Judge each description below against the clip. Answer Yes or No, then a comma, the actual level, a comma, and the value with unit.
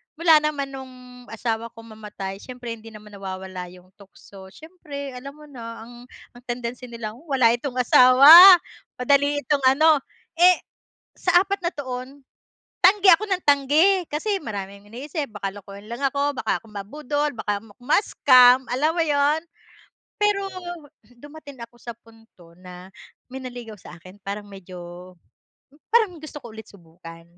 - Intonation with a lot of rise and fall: Yes, wide, 5.9 semitones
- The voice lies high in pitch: Yes, very high, 250 Hz